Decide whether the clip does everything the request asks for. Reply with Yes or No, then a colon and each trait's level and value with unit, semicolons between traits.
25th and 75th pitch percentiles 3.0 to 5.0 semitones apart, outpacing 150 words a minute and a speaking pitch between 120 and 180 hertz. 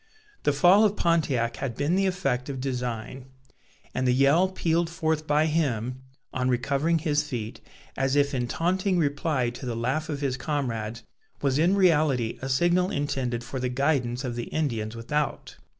Yes: average, 4.3 semitones; average, 170 wpm; medium, 140 Hz